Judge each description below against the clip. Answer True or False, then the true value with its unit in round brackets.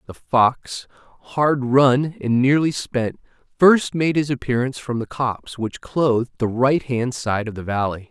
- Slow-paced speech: False (165 wpm)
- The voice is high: False (130 Hz)